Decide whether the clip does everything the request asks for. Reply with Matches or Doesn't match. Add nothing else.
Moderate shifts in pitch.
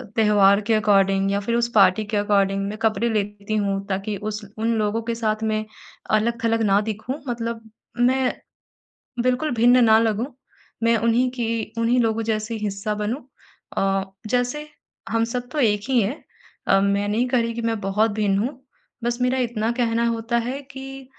Doesn't match